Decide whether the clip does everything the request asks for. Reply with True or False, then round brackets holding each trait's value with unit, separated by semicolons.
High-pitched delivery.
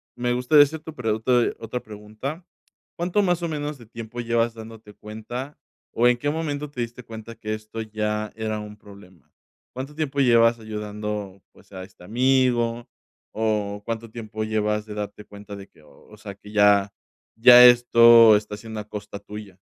False (110 Hz)